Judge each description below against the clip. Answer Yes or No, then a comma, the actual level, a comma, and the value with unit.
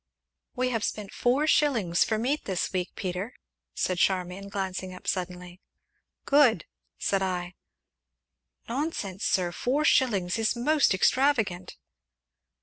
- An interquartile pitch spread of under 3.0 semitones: No, wide, 5.6 semitones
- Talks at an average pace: No, slow, 120 wpm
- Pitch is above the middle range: Yes, high, 195 Hz